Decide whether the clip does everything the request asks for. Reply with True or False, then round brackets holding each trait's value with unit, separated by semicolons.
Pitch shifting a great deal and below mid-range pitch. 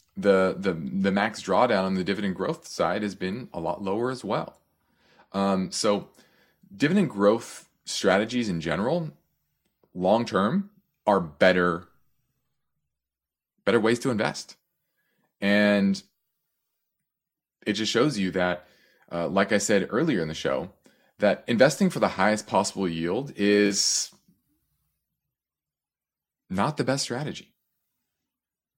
True (5.9 semitones; 100 Hz)